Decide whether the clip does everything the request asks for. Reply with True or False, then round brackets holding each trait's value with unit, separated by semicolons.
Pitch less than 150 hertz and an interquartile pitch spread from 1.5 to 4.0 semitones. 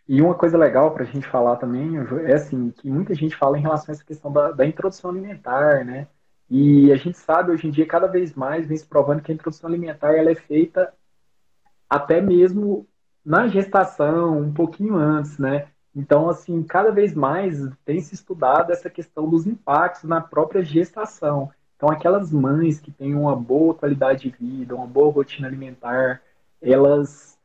False (155 Hz; 3.4 semitones)